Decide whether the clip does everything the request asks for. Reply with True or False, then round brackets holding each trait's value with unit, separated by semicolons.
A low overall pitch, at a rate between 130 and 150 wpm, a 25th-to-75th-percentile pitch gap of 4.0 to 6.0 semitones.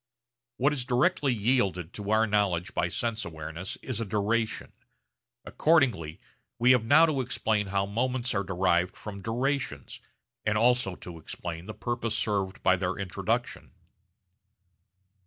True (105 Hz; 140 wpm; 4.7 semitones)